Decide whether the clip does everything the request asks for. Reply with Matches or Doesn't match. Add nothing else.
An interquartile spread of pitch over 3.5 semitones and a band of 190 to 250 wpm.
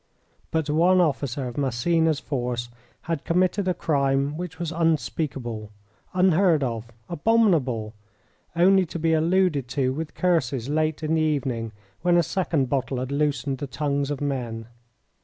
Doesn't match